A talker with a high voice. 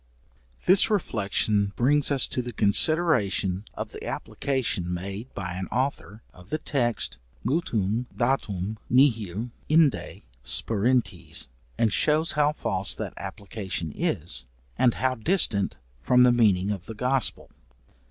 No: low, 115 Hz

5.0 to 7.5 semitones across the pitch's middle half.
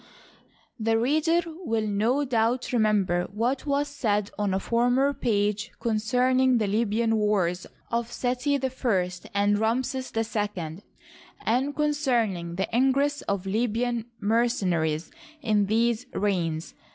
No: average, 3.9 semitones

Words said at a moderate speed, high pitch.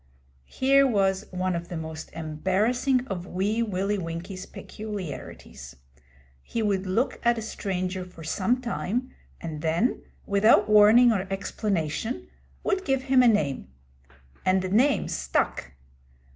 No: slow, 130 wpm; high, 195 Hz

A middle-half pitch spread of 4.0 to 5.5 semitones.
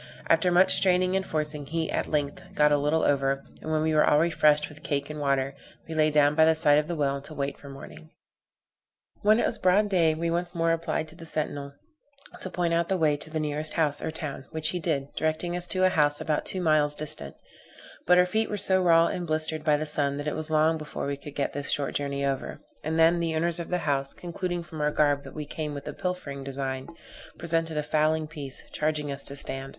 No: narrow, 2.5 semitones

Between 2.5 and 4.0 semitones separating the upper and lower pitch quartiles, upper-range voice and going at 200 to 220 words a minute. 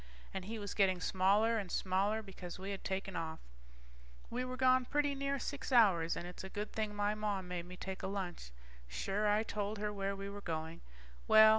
Yes: average, 2.8 semitones; high, 200 Hz; fast, 205 wpm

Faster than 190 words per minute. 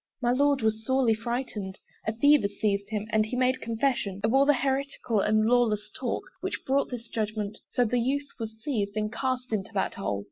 Yes: average, 200 wpm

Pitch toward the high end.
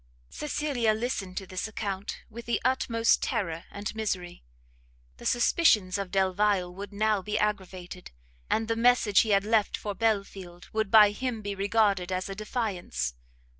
Yes: high, 205 Hz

